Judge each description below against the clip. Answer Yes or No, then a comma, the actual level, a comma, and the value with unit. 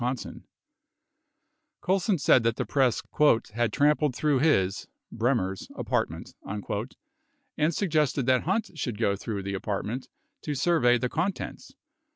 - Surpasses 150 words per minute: No, slow, 135 wpm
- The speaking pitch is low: Yes, low, 130 Hz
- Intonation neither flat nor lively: No, wide, 5.7 semitones